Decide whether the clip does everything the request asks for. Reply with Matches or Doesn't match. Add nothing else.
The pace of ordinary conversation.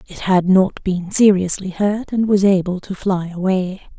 Matches